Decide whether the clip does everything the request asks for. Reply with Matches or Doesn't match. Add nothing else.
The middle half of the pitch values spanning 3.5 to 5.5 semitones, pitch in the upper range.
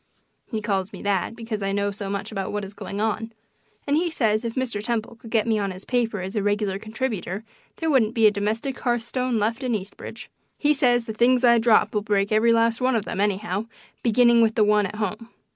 Doesn't match